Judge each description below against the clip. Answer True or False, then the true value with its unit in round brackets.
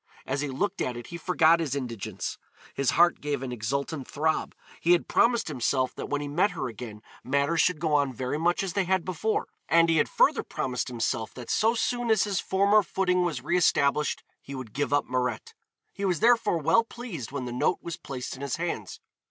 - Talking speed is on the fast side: True (215 wpm)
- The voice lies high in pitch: False (150 Hz)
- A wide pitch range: True (5.7 semitones)